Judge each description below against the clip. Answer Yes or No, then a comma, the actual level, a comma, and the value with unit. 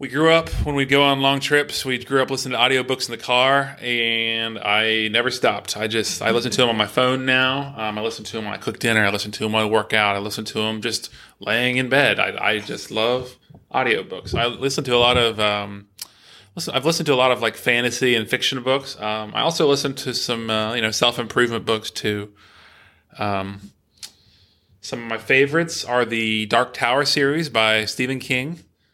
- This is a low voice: Yes, low, 120 Hz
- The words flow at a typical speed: No, fast, 220 wpm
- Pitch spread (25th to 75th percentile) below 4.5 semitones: Yes, average, 3.2 semitones